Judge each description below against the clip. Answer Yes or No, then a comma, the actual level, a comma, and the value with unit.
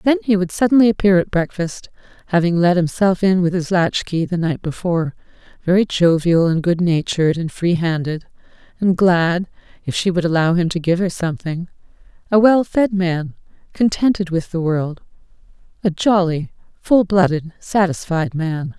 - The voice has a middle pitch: Yes, medium, 175 Hz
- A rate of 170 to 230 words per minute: No, average, 155 wpm